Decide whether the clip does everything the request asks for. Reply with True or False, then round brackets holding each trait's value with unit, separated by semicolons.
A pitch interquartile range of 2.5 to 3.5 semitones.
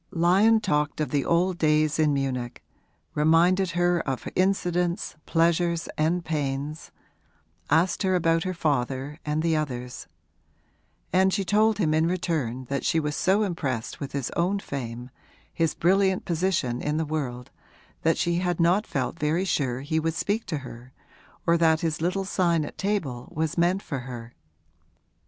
False (3.9 semitones)